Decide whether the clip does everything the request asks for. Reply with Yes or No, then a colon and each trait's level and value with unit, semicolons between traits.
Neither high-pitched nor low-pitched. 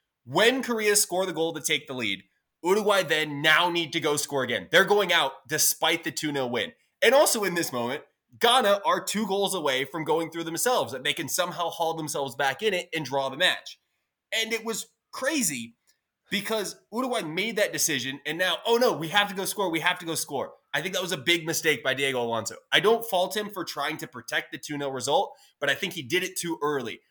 Yes: medium, 165 Hz